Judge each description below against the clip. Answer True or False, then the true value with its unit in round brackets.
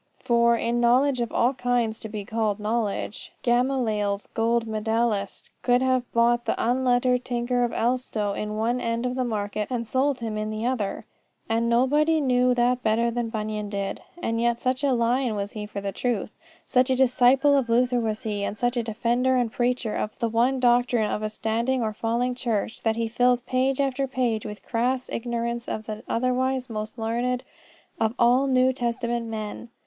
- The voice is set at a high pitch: True (235 Hz)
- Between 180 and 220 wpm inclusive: True (190 wpm)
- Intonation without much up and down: True (2.3 semitones)